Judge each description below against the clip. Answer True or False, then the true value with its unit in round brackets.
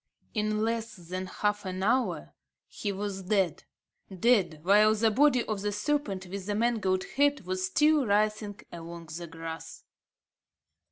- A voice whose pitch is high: True (205 Hz)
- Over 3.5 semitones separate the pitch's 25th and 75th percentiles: False (3.2 semitones)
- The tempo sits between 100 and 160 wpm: True (145 wpm)